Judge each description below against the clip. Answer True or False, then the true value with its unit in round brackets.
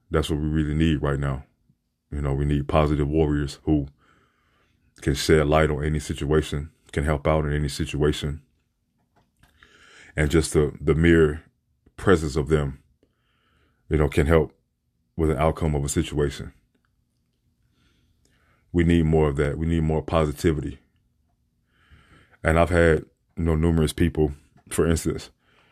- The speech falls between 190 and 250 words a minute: False (145 wpm)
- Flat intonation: True (1.8 semitones)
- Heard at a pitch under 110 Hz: True (75 Hz)